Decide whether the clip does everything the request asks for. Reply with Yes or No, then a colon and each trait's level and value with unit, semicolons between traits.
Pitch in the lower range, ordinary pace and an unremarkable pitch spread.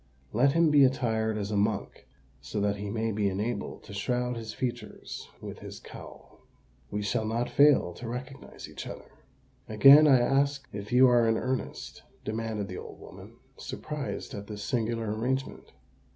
Yes: low, 115 Hz; average, 165 wpm; average, 3.9 semitones